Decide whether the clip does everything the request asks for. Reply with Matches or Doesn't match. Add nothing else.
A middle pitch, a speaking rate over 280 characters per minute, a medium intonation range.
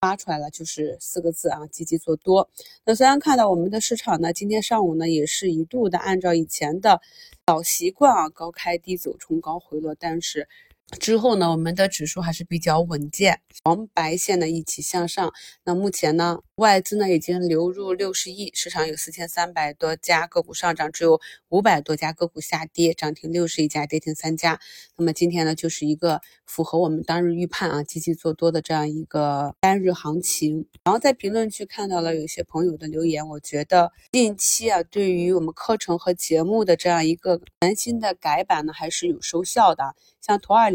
Matches